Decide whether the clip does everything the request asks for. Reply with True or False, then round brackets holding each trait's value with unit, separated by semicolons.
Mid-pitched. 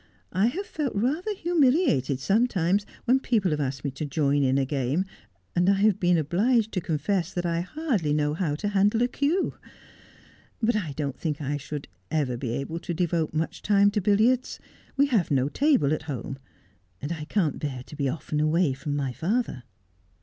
True (170 Hz)